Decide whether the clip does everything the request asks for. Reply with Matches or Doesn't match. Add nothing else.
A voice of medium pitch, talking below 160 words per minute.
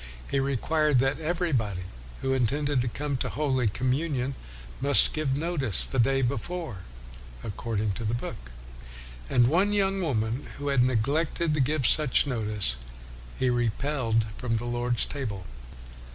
Doesn't match